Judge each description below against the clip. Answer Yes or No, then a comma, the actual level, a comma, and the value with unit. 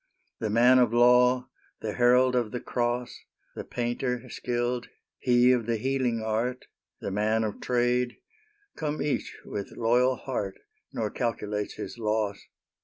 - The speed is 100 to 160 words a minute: Yes, average, 140 wpm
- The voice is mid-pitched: No, low, 120 Hz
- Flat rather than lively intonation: Yes, narrow, 2.0 semitones